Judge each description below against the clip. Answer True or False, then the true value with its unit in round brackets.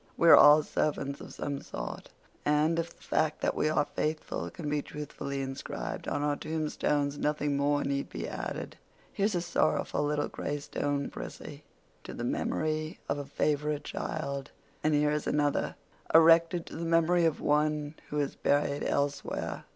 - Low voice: False (150 Hz)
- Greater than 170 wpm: False (165 wpm)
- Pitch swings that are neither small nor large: False (1.5 semitones)